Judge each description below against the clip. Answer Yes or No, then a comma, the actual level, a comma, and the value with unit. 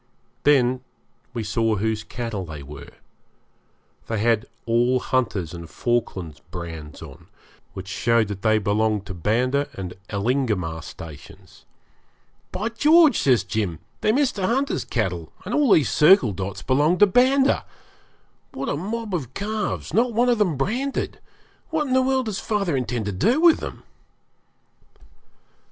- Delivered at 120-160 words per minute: Yes, average, 145 wpm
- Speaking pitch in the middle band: No, low, 125 Hz